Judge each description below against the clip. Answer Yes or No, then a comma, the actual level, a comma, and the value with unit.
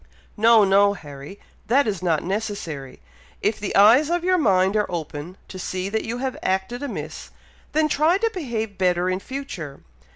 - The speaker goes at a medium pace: Yes, average, 170 wpm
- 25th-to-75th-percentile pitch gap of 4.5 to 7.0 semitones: Yes, wide, 5.4 semitones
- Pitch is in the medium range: No, high, 205 Hz